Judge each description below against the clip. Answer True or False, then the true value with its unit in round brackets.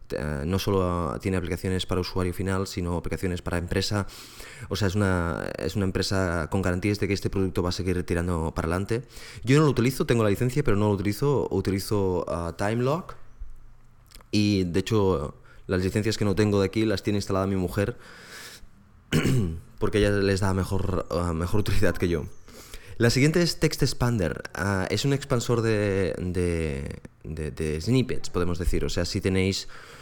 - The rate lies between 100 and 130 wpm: False (180 wpm)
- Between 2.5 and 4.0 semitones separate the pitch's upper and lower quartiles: True (3.3 semitones)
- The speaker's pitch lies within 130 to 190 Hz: False (95 Hz)